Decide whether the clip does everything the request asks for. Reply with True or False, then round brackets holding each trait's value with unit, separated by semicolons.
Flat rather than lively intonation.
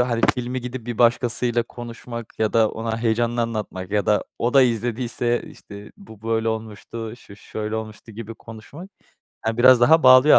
True (1.7 semitones)